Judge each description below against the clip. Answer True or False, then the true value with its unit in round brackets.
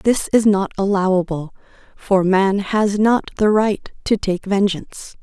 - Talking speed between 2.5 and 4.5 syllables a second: True (4.1 syllables/s)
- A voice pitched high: True (200 Hz)